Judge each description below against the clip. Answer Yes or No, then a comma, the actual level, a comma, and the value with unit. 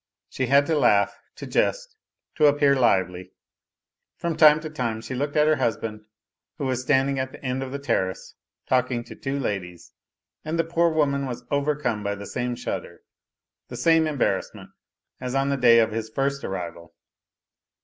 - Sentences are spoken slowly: No, average, 175 wpm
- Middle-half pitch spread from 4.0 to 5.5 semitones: Yes, average, 4.4 semitones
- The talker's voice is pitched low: Yes, low, 130 Hz